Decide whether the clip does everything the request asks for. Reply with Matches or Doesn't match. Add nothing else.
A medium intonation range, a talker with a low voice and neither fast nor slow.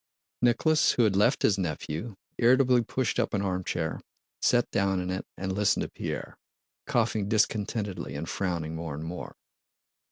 Matches